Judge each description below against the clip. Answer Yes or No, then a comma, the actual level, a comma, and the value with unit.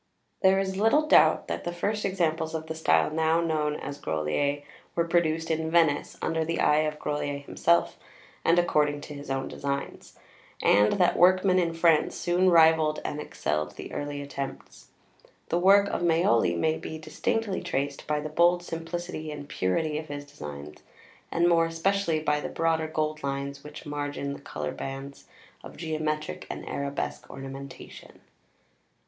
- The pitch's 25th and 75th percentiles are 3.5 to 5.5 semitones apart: No, average, 2.9 semitones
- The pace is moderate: Yes, average, 165 wpm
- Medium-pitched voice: Yes, medium, 155 Hz